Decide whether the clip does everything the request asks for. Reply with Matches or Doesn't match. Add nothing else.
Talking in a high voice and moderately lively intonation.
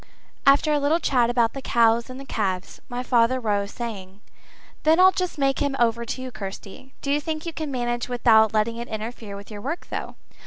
Matches